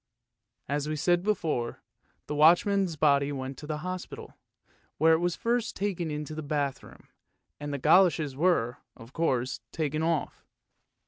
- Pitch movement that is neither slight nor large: Yes, average, 3.5 semitones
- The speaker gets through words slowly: No, average, 145 wpm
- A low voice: No, medium, 155 Hz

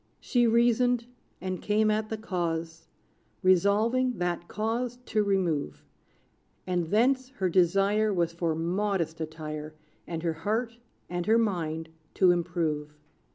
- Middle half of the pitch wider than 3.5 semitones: Yes, average, 4.8 semitones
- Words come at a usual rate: No, slow, 125 wpm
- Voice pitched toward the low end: No, medium, 185 Hz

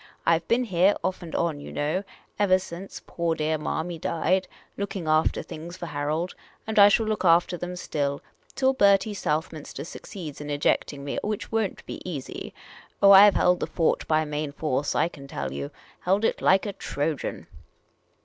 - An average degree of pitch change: Yes, average, 4.3 semitones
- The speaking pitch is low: No, medium, 170 Hz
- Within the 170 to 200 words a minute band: Yes, average, 185 wpm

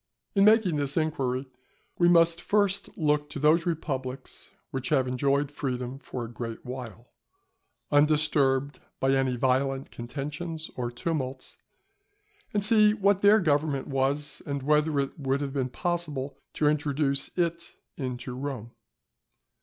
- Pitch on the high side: No, medium, 140 Hz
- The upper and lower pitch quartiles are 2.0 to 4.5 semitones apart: Yes, average, 3.4 semitones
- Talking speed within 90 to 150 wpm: Yes, slow, 135 wpm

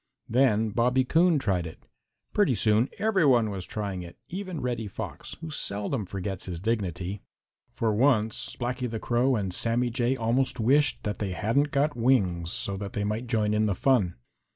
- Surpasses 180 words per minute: No, average, 175 wpm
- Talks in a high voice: No, low, 115 Hz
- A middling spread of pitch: Yes, average, 4.4 semitones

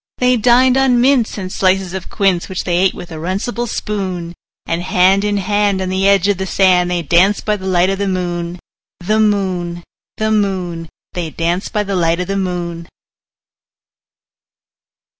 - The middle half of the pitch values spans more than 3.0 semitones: No, average, 2.7 semitones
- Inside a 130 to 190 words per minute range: Yes, average, 180 wpm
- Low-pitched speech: No, high, 190 Hz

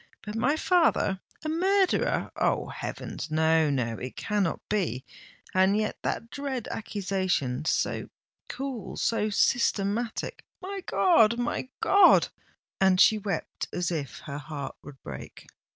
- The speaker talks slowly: Yes, slow, 100 wpm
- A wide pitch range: Yes, wide, 7.3 semitones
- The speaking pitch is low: No, high, 205 Hz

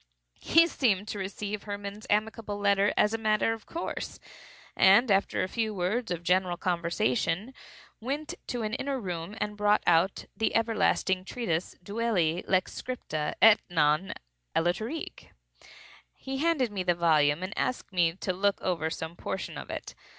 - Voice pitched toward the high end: Yes, high, 200 Hz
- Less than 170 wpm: Yes, average, 155 wpm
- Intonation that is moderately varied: Yes, average, 4.1 semitones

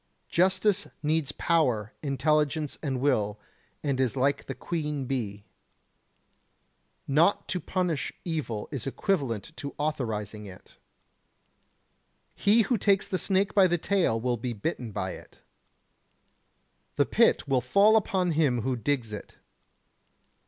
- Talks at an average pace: No, slow, 130 wpm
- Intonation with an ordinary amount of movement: No, wide, 6.3 semitones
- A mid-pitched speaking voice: Yes, medium, 145 Hz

